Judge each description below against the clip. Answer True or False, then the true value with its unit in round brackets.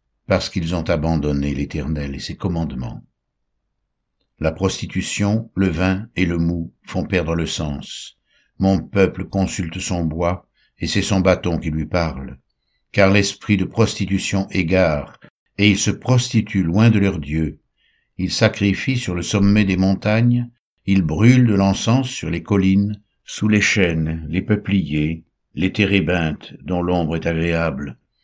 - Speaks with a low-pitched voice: True (95 Hz)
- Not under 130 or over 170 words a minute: True (145 wpm)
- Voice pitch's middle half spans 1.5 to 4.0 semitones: True (3.6 semitones)